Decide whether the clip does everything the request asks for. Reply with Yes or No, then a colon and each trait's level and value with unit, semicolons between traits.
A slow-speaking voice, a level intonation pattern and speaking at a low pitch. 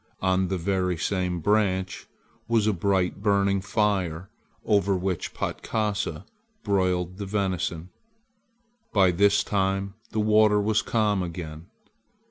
Yes: slow, 115 wpm; narrow, 2.2 semitones; very low, 95 Hz